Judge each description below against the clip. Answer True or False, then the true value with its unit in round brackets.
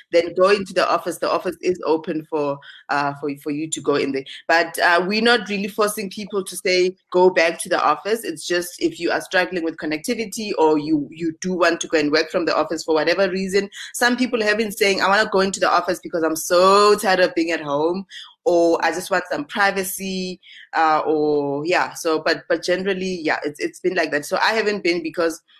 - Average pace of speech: False (230 wpm)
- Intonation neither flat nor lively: True (3.7 semitones)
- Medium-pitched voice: True (180 Hz)